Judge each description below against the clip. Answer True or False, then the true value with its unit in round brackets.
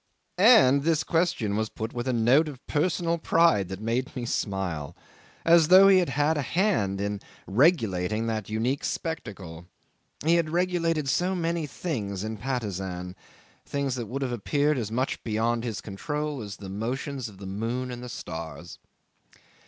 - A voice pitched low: True (125 Hz)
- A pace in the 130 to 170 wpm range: True (165 wpm)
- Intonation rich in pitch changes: True (7.1 semitones)